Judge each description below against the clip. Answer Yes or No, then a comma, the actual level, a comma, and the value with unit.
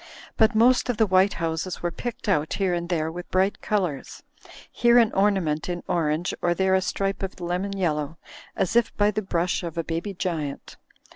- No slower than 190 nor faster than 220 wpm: Yes, average, 195 wpm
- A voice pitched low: No, medium, 185 Hz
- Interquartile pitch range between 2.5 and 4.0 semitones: Yes, average, 3.2 semitones